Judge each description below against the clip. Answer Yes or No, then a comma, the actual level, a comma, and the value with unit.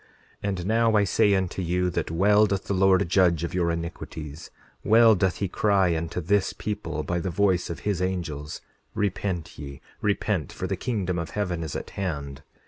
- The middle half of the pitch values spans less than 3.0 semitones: No, average, 3.3 semitones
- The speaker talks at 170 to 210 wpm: Yes, average, 190 wpm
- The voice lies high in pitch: No, very low, 90 Hz